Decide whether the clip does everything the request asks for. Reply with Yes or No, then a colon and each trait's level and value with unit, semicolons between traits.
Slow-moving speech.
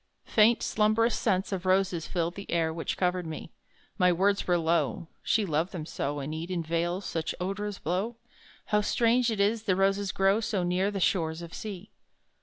No: average, 185 wpm